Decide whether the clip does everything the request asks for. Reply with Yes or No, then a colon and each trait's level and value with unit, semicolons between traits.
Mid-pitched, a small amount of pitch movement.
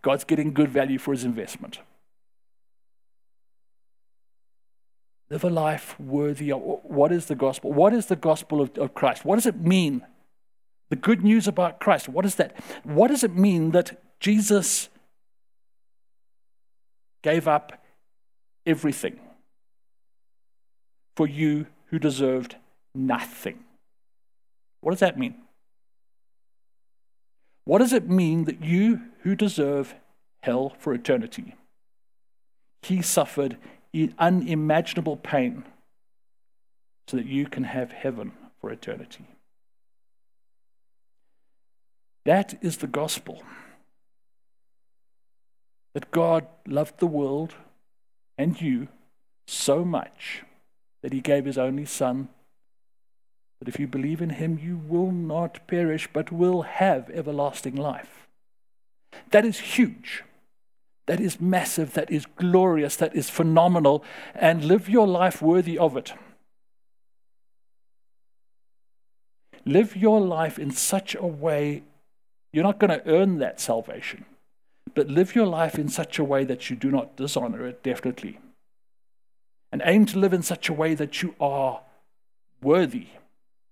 No: medium, 160 Hz; average, 4.4 semitones